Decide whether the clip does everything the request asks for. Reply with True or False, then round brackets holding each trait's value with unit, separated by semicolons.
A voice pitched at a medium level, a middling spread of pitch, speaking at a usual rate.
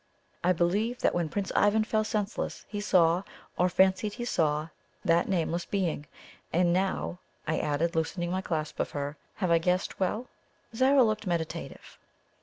True (180 Hz; 3.7 semitones; 160 wpm)